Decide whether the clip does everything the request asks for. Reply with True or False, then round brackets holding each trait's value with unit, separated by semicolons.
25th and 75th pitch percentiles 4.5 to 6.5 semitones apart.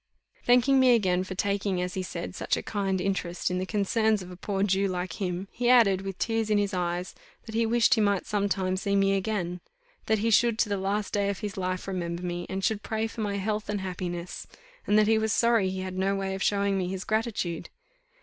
False (2.6 semitones)